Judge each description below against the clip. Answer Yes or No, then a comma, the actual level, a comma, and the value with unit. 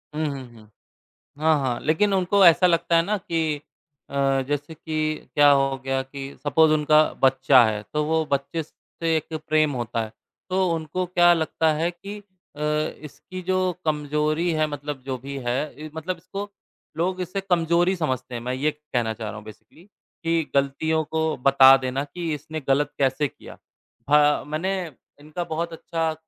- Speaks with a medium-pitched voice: Yes, medium, 155 Hz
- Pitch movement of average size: Yes, average, 3.3 semitones